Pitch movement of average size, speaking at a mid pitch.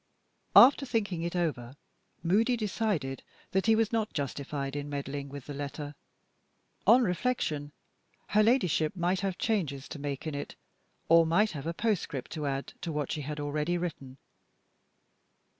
No: wide, 6.2 semitones; medium, 160 Hz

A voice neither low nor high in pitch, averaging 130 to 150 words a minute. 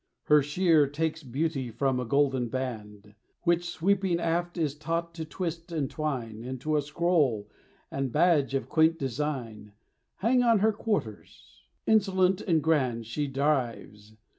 Yes: medium, 150 Hz; average, 140 wpm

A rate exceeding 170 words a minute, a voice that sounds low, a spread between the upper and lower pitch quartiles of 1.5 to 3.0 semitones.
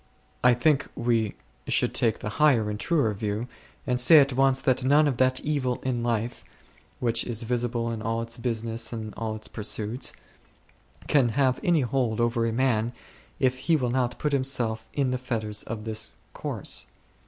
Yes: average, 180 wpm; low, 120 Hz; narrow, 2.5 semitones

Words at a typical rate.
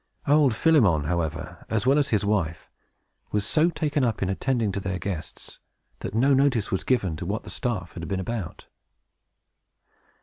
Yes: average, 170 wpm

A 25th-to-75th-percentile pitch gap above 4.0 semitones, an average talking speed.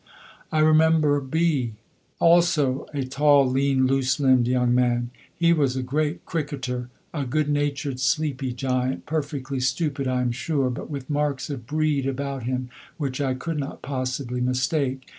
No: narrow, 2.6 semitones; average, 155 wpm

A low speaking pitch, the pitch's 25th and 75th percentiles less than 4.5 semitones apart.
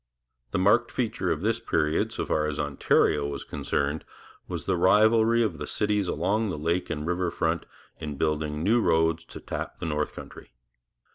No: very low, 85 Hz; wide, 5.5 semitones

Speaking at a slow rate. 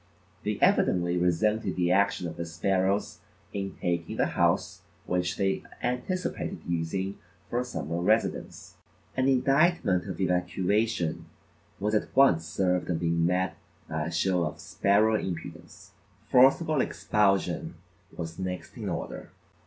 Yes: slow, 130 wpm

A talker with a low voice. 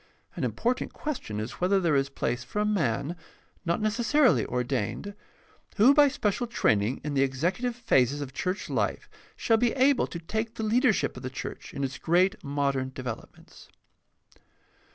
No: medium, 170 Hz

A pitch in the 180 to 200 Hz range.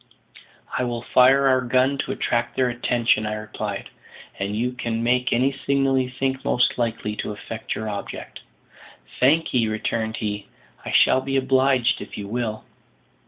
No: low, 120 Hz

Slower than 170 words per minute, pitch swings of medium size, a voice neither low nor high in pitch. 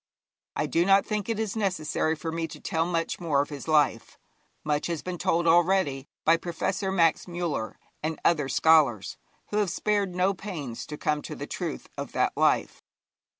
No: average, 185 wpm; average, 3.8 semitones; medium, 165 Hz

